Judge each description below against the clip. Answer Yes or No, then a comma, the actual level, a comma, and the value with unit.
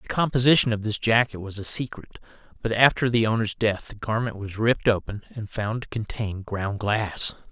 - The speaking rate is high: No, average, 190 wpm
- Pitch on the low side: Yes, low, 110 Hz